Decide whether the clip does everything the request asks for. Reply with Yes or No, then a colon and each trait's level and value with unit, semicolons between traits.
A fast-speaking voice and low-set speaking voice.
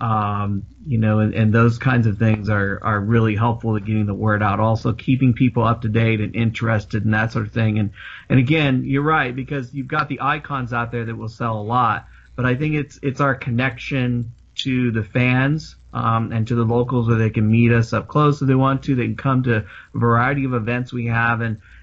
Yes: fast, 235 wpm; low, 115 Hz